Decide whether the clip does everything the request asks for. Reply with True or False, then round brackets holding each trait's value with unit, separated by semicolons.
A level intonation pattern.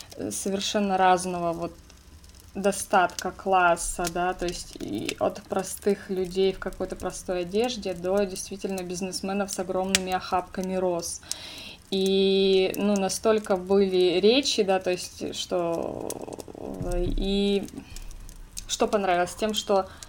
True (1.9 semitones)